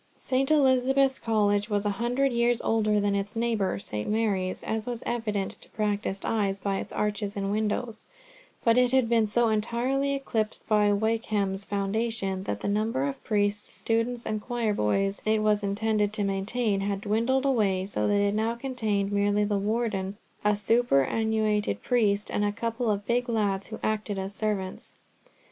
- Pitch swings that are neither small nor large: No, narrow, 2.3 semitones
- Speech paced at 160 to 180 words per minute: Yes, average, 170 wpm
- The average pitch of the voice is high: Yes, high, 215 Hz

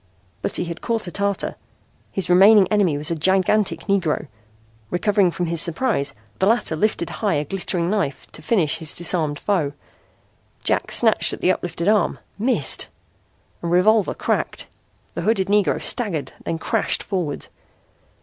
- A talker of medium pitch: Yes, medium, 180 Hz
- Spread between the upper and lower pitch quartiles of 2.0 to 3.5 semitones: No, average, 4.0 semitones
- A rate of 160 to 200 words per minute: No, average, 150 wpm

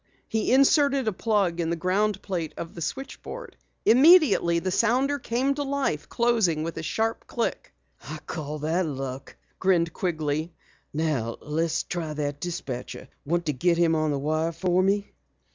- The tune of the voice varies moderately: No, wide, 6.2 semitones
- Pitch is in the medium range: Yes, medium, 170 Hz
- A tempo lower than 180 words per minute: Yes, average, 160 wpm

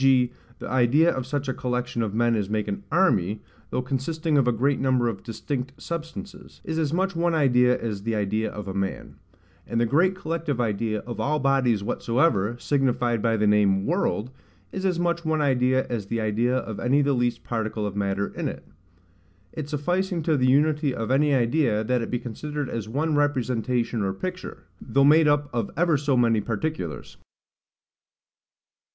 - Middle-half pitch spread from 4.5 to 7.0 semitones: Yes, average, 4.9 semitones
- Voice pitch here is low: Yes, low, 125 Hz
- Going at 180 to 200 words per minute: Yes, average, 185 wpm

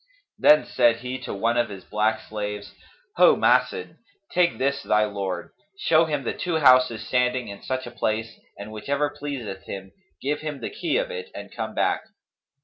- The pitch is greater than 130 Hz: No, low, 120 Hz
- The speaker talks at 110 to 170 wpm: No, average, 180 wpm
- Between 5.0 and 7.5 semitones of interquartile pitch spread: Yes, wide, 5.4 semitones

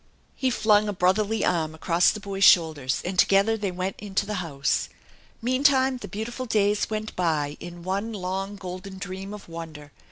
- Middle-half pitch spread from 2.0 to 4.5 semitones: Yes, average, 3.4 semitones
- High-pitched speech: Yes, high, 195 Hz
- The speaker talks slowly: No, average, 170 wpm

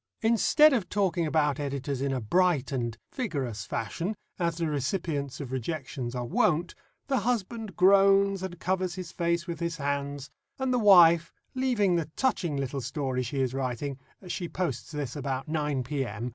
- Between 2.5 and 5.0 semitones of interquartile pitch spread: No, wide, 5.5 semitones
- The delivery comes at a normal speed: Yes, average, 165 wpm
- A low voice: No, medium, 155 Hz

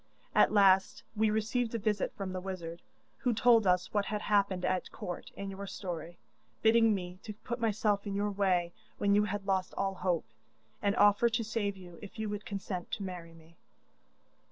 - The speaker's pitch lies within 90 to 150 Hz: No, high, 200 Hz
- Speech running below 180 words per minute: No, average, 190 wpm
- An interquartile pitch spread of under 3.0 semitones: Yes, narrow, 2.5 semitones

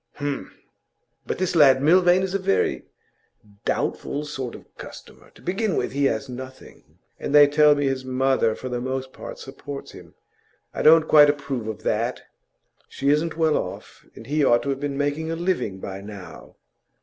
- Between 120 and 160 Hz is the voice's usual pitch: Yes, medium, 140 Hz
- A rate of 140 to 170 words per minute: No, average, 180 wpm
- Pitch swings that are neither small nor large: Yes, average, 3.1 semitones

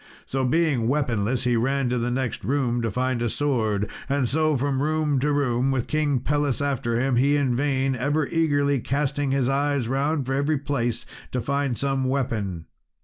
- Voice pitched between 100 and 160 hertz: Yes, low, 135 Hz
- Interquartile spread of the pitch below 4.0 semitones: Yes, average, 2.8 semitones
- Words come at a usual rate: Yes, average, 180 wpm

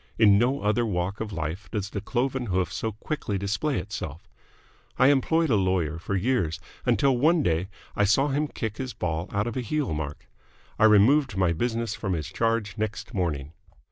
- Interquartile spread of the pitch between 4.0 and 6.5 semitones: Yes, average, 5.2 semitones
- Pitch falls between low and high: No, low, 105 Hz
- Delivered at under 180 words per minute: No, average, 185 wpm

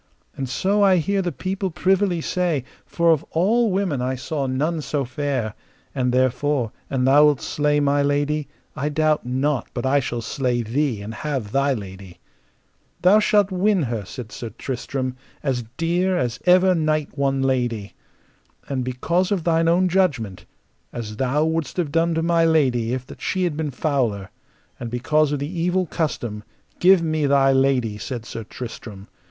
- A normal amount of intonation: Yes, average, 4.9 semitones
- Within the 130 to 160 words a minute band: No, average, 170 wpm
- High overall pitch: No, medium, 145 Hz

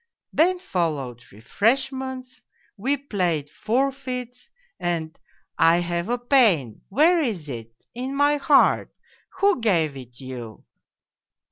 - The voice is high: Yes, high, 215 Hz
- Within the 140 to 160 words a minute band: Yes, average, 145 wpm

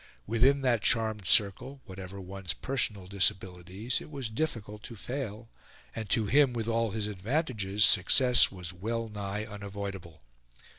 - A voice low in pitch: Yes, low, 105 Hz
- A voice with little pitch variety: No, average, 3.4 semitones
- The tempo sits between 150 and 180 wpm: No, average, 140 wpm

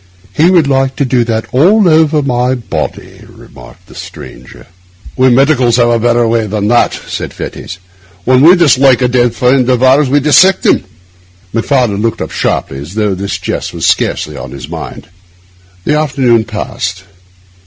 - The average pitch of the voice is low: Yes, low, 125 Hz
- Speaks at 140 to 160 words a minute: No, average, 170 wpm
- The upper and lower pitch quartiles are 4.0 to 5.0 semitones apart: No, average, 3.6 semitones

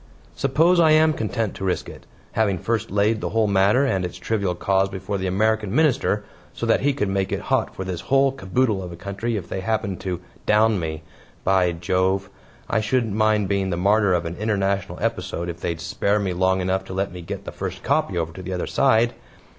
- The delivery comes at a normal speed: No, fast, 220 wpm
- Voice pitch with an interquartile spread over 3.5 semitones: No, average, 3.1 semitones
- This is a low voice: Yes, low, 100 Hz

